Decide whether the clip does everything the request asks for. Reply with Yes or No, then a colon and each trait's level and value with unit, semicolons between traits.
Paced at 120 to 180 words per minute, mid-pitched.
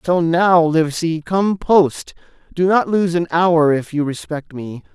Yes: average, 170 wpm; medium, 165 Hz